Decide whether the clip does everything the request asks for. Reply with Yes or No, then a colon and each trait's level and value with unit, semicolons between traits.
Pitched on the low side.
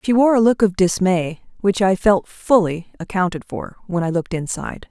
No: high, 190 Hz